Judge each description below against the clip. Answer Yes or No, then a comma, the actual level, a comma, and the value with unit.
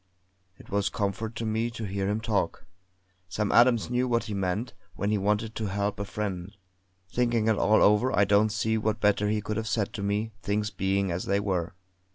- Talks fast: Yes, fast, 210 wpm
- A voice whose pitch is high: No, low, 105 Hz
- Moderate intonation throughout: No, narrow, 1.8 semitones